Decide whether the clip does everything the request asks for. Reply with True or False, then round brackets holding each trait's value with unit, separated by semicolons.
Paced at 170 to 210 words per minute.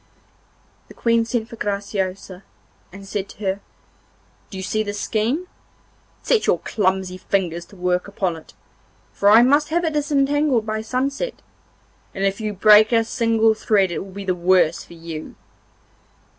False (160 wpm)